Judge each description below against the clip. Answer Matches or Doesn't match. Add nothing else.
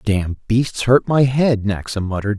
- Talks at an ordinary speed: Matches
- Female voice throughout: Doesn't match